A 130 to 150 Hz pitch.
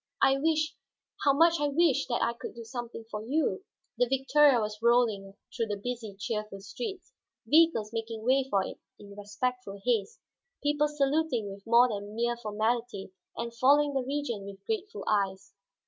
No: high, 235 Hz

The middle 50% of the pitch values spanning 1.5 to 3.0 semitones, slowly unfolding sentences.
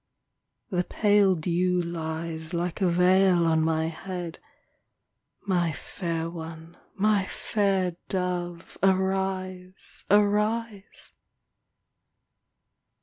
Yes: narrow, 2.4 semitones; slow, 85 wpm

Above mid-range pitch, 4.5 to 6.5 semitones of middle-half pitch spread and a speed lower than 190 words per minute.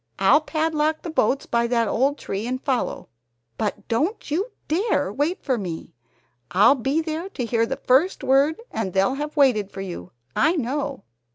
Yes: very high, 270 Hz; wide, 5.4 semitones; average, 175 wpm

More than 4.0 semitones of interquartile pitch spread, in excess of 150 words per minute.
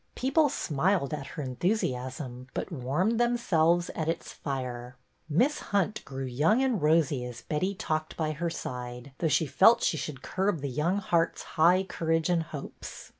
Yes: wide, 5.5 semitones; average, 165 wpm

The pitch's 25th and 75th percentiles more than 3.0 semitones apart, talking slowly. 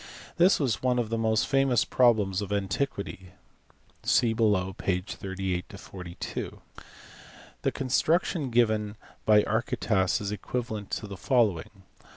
Yes: average, 3.9 semitones; slow, 125 wpm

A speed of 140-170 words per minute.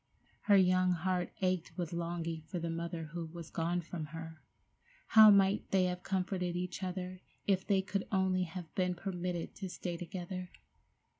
Yes: average, 165 wpm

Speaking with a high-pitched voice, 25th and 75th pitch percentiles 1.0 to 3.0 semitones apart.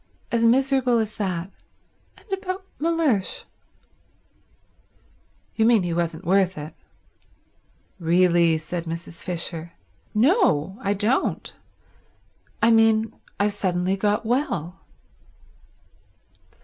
No: high, 200 Hz; wide, 5.4 semitones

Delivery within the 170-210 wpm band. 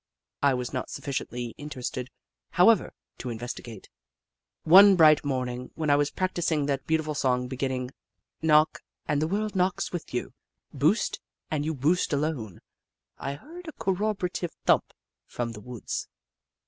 No: average, 145 wpm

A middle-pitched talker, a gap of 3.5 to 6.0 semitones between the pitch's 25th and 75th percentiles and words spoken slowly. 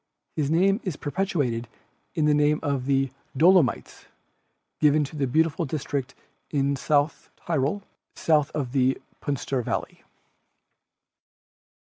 No: medium, 145 Hz; average, 2.8 semitones; slow, 115 wpm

